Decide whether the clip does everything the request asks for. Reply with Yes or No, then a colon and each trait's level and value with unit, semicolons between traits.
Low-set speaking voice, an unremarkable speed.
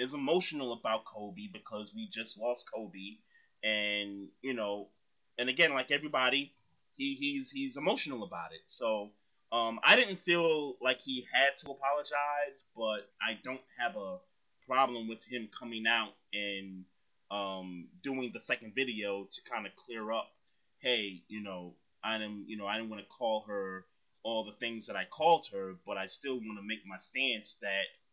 Yes: low, 115 Hz; average, 175 wpm